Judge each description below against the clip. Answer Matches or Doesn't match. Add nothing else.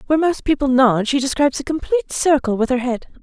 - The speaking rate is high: Matches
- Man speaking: Doesn't match